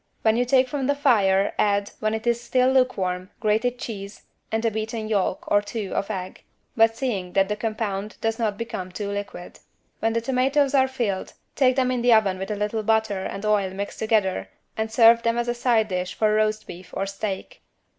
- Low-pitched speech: No, high, 220 Hz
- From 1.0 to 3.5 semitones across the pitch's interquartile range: Yes, average, 3.1 semitones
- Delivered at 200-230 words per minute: Yes, fast, 205 wpm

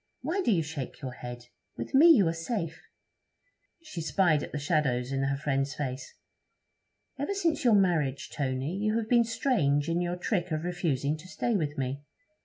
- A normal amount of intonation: No, wide, 6.9 semitones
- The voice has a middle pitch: Yes, medium, 160 Hz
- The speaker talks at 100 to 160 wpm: No, average, 185 wpm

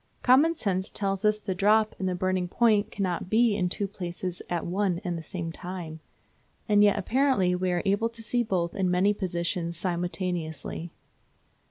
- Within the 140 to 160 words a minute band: No, average, 175 wpm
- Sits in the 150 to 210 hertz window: Yes, medium, 185 Hz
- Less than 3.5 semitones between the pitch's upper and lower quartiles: Yes, average, 2.8 semitones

